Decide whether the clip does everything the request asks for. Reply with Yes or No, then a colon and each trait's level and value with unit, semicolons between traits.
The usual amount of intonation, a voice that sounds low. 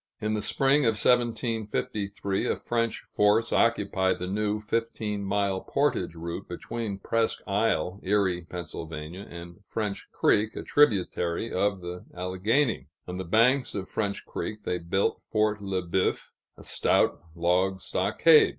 Yes: average, 3.4 semitones; low, 100 Hz